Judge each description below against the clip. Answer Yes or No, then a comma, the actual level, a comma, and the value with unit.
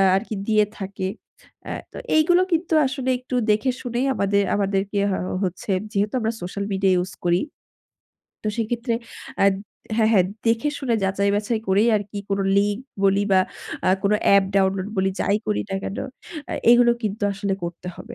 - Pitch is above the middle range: Yes, high, 205 Hz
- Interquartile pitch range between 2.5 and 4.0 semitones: Yes, average, 3.0 semitones